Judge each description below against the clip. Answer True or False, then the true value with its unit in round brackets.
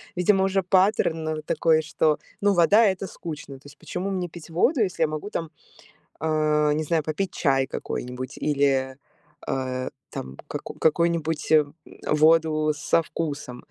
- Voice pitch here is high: False (155 Hz)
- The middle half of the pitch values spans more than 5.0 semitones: False (2.9 semitones)